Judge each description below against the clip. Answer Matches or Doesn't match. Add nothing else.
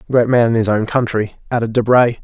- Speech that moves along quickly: Matches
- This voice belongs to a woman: Doesn't match